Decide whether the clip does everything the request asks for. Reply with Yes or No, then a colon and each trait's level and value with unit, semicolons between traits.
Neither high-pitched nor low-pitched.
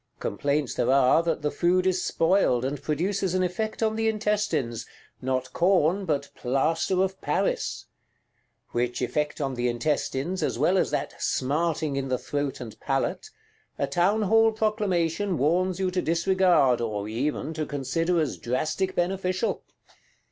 Yes: medium, 165 Hz